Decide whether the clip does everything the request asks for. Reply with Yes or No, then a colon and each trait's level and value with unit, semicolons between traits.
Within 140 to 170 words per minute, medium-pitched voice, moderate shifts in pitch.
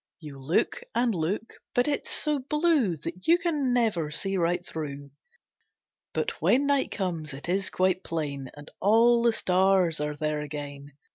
No: average, 160 wpm; medium, 180 Hz; wide, 7.9 semitones